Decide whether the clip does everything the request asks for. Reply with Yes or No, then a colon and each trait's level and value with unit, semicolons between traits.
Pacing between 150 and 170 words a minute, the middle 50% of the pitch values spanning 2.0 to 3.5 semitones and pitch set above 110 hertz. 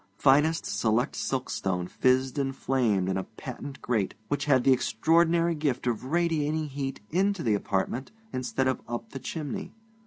No: average, 155 wpm; average, 4.3 semitones; low, 135 Hz